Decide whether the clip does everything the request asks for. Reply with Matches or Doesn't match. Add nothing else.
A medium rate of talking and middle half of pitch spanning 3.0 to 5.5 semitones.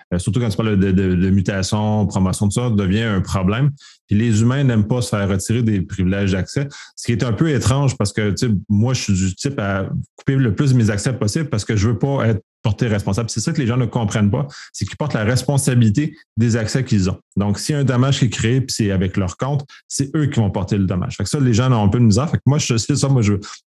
Doesn't match